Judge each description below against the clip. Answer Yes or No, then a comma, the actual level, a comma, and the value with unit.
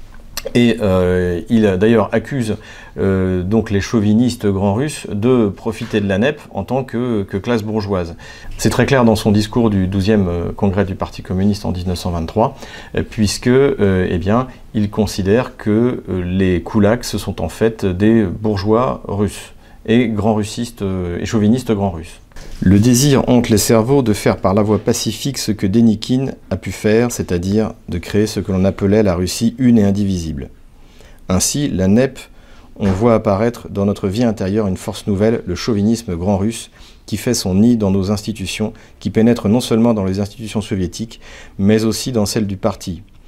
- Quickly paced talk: No, average, 170 wpm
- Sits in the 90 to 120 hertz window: Yes, low, 105 Hz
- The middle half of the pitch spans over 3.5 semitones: No, average, 2.8 semitones